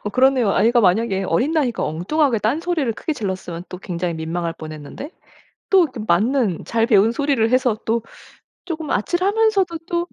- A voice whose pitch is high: Yes, high, 230 Hz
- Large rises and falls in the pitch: Yes, wide, 8.1 semitones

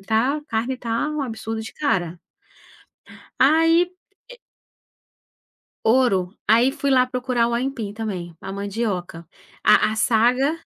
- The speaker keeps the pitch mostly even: No, average, 3.7 semitones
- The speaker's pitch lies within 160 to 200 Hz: No, high, 235 Hz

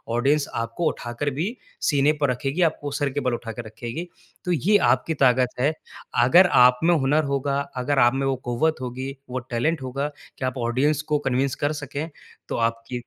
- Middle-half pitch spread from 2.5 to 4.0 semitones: Yes, average, 3.0 semitones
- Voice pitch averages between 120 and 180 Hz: Yes, low, 135 Hz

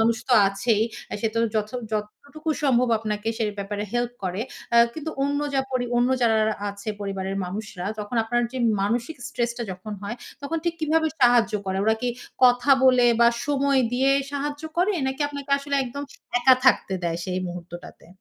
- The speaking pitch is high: Yes, high, 240 Hz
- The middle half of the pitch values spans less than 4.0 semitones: No, average, 4.7 semitones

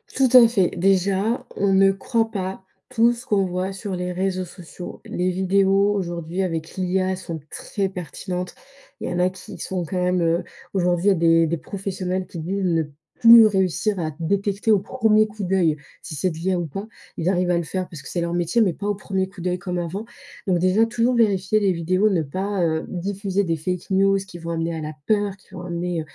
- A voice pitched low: No, medium, 185 Hz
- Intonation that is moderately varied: No, narrow, 2.2 semitones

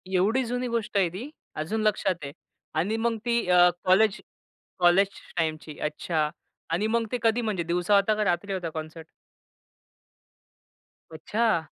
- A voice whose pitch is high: Yes, high, 195 Hz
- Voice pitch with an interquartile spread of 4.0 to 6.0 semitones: Yes, average, 4.9 semitones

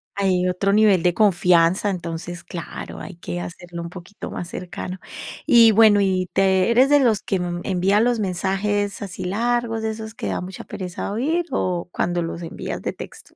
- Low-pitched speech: No, high, 190 Hz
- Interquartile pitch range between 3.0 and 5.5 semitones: Yes, average, 3.4 semitones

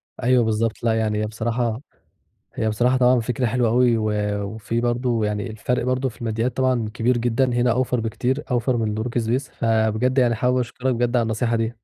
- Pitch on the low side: Yes, low, 120 Hz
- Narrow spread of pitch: Yes, narrow, 2.0 semitones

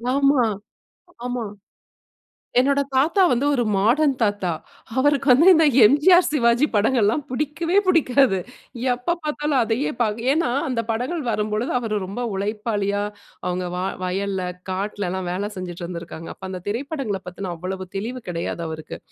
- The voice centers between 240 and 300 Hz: No, high, 225 Hz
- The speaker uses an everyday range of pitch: No, wide, 6.3 semitones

